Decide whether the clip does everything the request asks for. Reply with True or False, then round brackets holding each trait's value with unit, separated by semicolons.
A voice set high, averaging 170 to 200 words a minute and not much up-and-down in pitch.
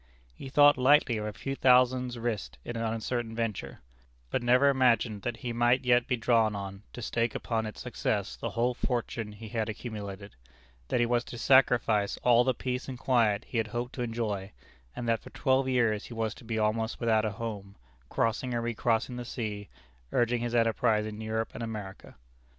False (115 Hz; 195 wpm; 2.2 semitones)